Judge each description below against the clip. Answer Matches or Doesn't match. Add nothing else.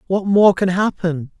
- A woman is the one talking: Doesn't match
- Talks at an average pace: Matches